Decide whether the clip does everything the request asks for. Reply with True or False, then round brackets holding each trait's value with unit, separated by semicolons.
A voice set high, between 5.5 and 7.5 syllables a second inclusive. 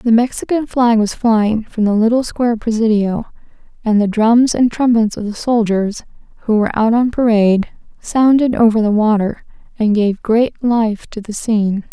False (225 Hz; 4.9 syllables/s)